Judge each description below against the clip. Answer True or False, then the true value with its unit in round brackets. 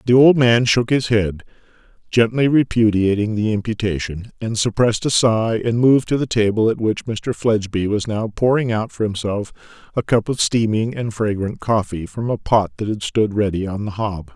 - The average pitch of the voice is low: True (110 Hz)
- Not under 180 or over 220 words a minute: True (190 wpm)